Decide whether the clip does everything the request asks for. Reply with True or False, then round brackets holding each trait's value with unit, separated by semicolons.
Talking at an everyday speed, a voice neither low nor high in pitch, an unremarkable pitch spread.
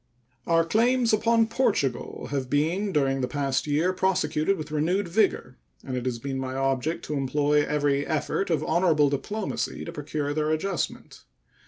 True (160 wpm; 150 Hz; 5.0 semitones)